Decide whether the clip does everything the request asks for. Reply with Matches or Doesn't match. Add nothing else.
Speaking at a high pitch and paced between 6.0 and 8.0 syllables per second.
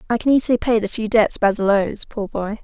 Doesn't match